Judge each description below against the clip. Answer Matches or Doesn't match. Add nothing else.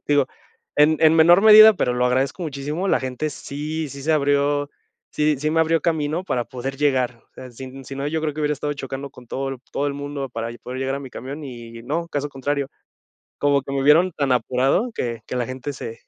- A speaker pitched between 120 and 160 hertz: Matches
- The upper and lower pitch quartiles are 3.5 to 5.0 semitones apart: Doesn't match